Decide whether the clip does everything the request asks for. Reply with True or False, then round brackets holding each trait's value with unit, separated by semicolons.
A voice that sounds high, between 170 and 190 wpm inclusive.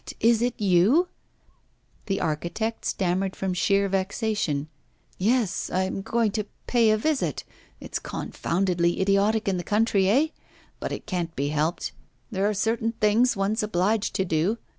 False (200 Hz; 155 wpm)